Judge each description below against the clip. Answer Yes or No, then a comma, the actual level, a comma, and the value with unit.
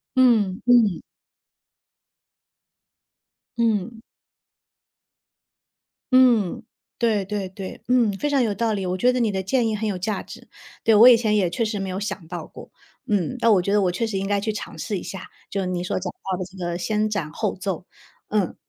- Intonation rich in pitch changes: No, average, 3.2 semitones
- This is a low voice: No, high, 205 Hz